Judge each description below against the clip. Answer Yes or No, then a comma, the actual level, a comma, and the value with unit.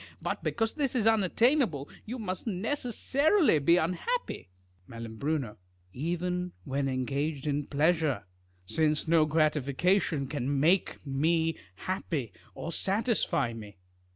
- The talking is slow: Yes, slow, 115 wpm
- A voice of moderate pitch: Yes, medium, 160 Hz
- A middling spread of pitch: No, wide, 5.7 semitones